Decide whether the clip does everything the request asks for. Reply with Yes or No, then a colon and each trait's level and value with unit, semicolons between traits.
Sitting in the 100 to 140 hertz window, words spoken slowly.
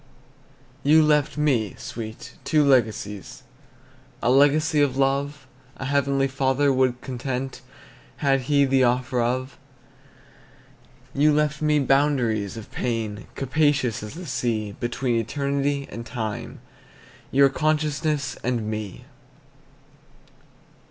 Yes: low, 135 Hz; slow, 110 wpm